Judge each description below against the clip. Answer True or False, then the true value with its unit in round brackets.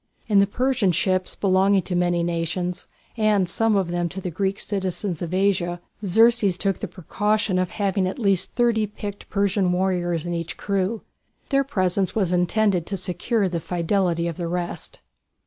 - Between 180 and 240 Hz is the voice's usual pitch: True (190 Hz)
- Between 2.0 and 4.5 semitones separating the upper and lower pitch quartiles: True (2.5 semitones)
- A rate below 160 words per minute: False (170 wpm)